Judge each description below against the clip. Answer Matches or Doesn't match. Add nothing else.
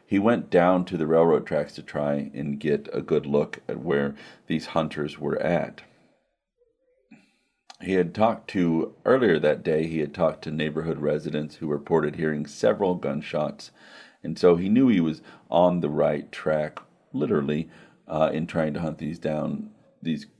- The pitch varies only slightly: Matches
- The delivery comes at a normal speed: Matches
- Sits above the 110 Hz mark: Doesn't match